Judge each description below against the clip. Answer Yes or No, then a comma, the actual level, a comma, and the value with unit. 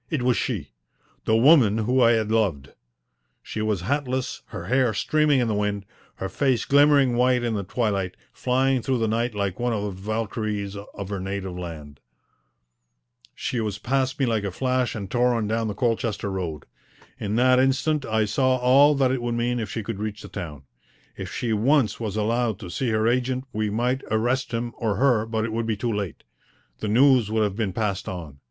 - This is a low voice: Yes, low, 115 Hz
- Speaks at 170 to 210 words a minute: Yes, average, 200 wpm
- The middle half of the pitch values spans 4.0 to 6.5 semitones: No, average, 3.6 semitones